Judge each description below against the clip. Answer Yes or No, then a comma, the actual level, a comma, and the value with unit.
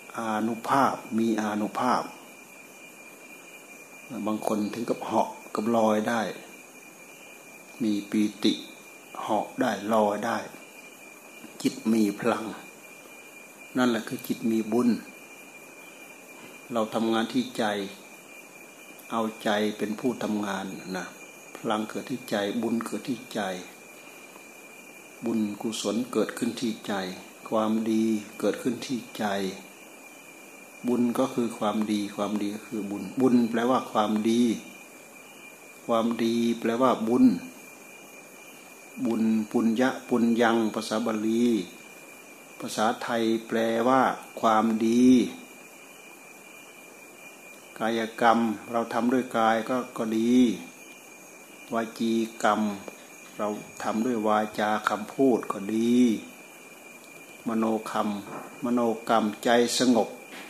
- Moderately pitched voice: No, low, 115 Hz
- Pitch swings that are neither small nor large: No, narrow, 1.6 semitones